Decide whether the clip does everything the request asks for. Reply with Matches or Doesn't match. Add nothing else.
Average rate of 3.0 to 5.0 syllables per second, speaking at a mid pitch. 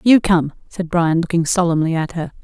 Doesn't match